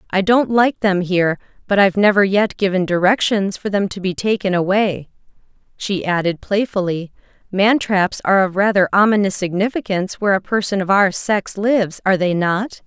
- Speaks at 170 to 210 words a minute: Yes, average, 175 wpm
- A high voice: Yes, high, 195 Hz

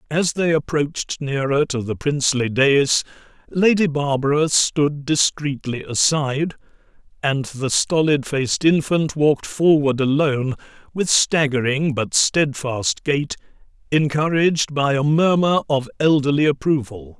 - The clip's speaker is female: No, male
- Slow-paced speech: Yes, slow, 115 wpm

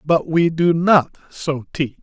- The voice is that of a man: Yes, male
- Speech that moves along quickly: No, average, 180 wpm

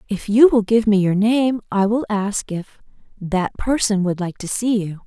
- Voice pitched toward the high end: Yes, high, 210 Hz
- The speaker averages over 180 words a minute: Yes, average, 200 wpm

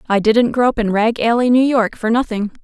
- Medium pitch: No, high, 230 Hz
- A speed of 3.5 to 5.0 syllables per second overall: No, 5.5 syllables/s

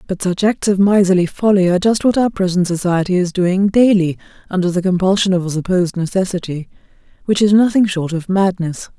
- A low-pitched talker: No, medium, 185 Hz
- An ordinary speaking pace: Yes, average, 185 wpm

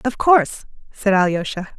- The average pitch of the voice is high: Yes, high, 210 Hz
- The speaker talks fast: No, slow, 135 wpm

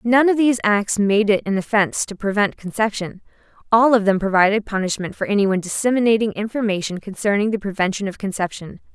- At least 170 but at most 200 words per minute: No, average, 160 wpm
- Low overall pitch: No, high, 205 Hz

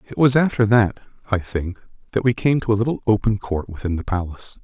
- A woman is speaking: No, male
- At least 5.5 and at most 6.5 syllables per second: Yes, 5.9 syllables/s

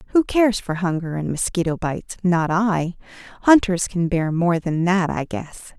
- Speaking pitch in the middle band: Yes, medium, 180 Hz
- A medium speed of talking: Yes, average, 175 wpm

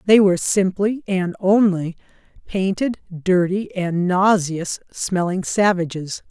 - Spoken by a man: No, female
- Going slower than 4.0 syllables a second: Yes, 3.7 syllables/s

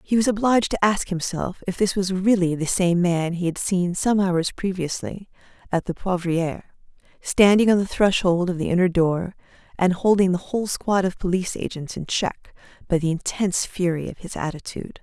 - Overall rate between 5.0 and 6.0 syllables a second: Yes, 5.3 syllables/s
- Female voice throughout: Yes, female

